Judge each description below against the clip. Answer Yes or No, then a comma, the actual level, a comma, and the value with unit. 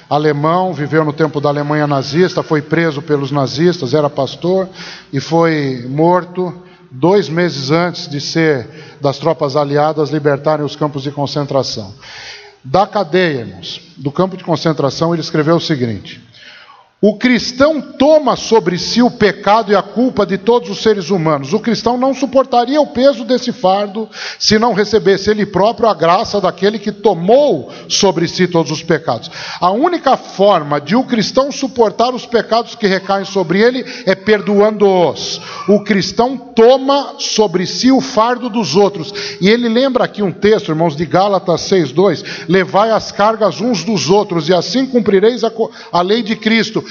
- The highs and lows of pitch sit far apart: Yes, wide, 5.7 semitones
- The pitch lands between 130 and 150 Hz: No, high, 190 Hz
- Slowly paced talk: No, average, 160 wpm